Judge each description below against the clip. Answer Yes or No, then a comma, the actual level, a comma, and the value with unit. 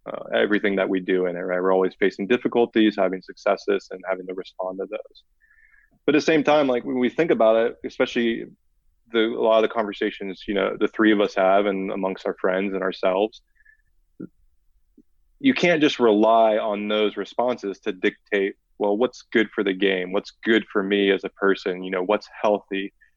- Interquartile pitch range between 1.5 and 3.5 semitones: No, average, 4.2 semitones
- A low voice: Yes, low, 105 Hz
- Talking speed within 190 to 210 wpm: Yes, average, 200 wpm